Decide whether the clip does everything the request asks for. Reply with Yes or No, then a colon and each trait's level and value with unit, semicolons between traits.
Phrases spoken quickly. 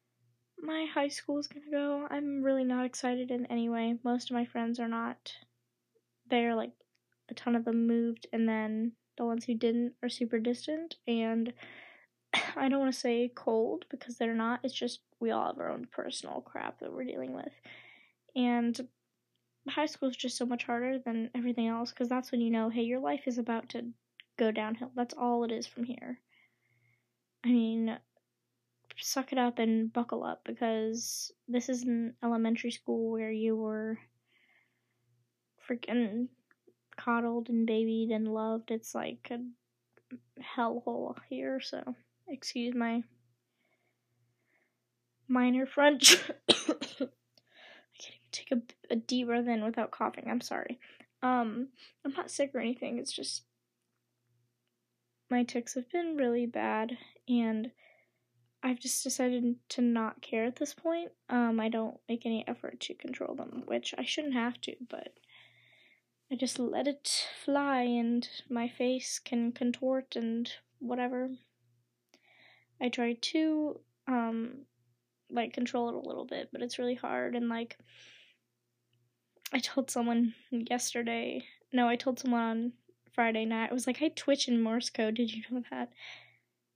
No: average, 155 wpm